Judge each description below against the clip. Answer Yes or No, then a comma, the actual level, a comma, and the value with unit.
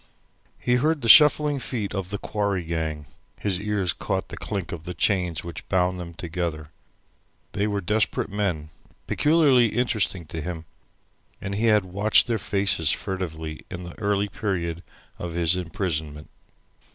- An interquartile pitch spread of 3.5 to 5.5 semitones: Yes, average, 3.8 semitones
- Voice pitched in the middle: No, very low, 95 Hz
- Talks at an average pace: Yes, average, 150 wpm